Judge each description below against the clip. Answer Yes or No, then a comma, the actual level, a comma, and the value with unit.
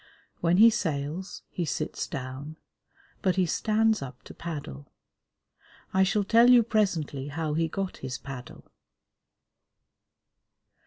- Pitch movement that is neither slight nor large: No, wide, 6.2 semitones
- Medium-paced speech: No, slow, 120 wpm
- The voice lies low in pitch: No, medium, 165 Hz